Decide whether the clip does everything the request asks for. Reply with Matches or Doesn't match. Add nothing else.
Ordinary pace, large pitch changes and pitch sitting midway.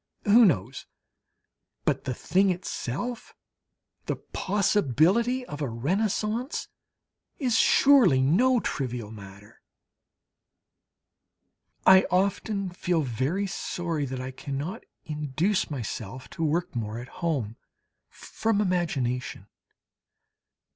Doesn't match